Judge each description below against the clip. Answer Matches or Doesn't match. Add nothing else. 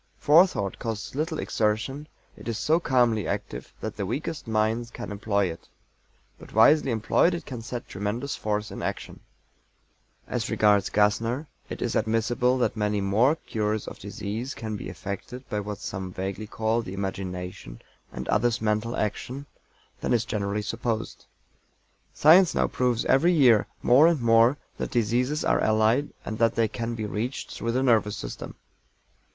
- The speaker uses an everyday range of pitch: Matches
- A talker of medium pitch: Doesn't match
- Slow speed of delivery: Doesn't match